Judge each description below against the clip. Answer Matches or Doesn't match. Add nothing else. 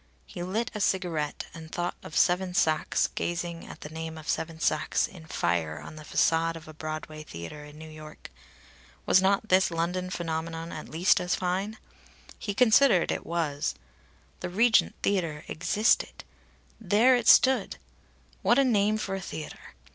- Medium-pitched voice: Matches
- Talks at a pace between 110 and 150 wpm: Doesn't match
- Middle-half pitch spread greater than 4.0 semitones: Doesn't match